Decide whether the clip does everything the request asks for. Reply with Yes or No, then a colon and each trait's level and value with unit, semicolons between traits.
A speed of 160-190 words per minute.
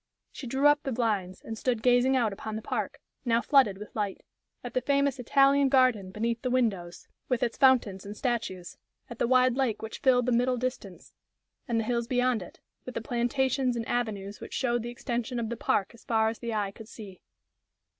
No: fast, 205 wpm